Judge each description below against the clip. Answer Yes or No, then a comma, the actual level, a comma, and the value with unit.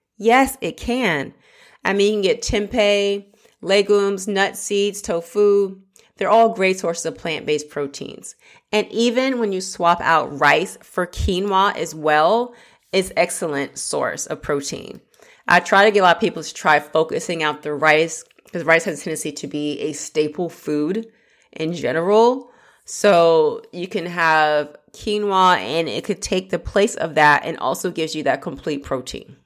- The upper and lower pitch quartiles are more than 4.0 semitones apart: Yes, average, 4.6 semitones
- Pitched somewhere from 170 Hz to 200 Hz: Yes, high, 190 Hz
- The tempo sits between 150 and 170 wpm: Yes, average, 165 wpm